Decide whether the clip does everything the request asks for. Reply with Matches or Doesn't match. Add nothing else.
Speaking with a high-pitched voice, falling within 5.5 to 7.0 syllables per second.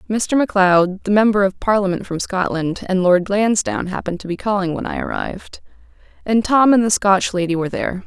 Matches